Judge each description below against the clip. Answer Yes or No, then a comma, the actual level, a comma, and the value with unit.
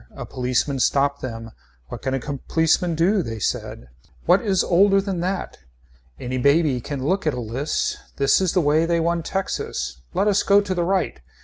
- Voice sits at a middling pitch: Yes, medium, 160 Hz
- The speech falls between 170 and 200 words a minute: Yes, average, 190 wpm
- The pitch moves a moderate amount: No, wide, 6.1 semitones